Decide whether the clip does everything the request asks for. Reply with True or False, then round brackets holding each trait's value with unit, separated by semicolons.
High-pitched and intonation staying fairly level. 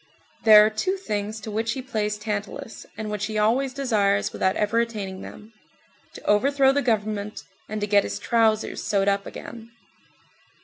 True (215 Hz; 1.9 semitones)